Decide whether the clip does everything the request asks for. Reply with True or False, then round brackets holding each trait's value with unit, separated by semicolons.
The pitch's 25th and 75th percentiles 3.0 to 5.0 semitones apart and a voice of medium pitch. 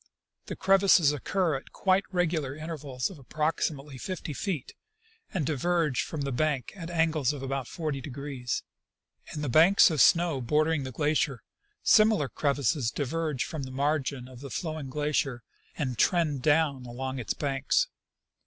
True (3.4 semitones; 145 Hz)